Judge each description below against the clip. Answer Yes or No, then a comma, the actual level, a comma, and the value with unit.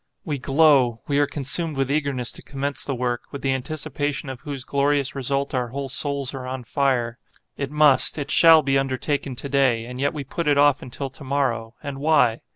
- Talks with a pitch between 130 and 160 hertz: Yes, medium, 140 Hz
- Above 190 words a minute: Yes, fast, 205 wpm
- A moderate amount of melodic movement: No, narrow, 2.0 semitones